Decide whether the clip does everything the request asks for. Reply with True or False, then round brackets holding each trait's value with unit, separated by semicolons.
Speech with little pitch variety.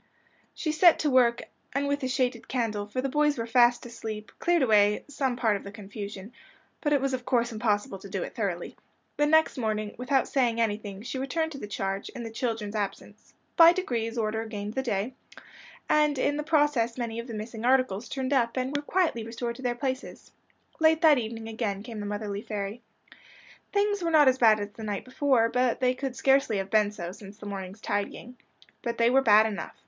False (4.2 semitones)